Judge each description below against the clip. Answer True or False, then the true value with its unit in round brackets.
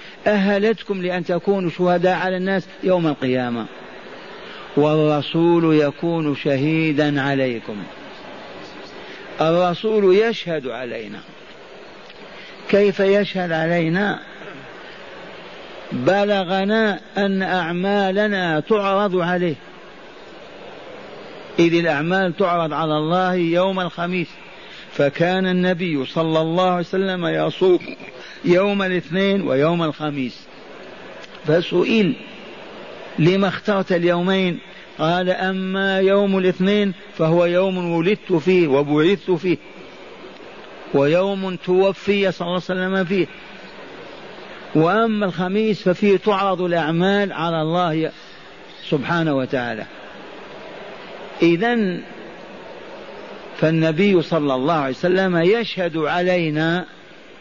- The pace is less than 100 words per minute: True (85 wpm)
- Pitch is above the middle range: False (180 Hz)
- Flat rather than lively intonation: False (3.0 semitones)